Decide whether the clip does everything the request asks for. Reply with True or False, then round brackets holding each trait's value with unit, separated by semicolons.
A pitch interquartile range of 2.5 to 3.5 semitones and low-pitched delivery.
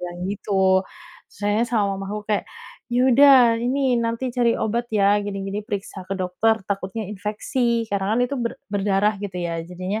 False (3.0 semitones; 205 Hz)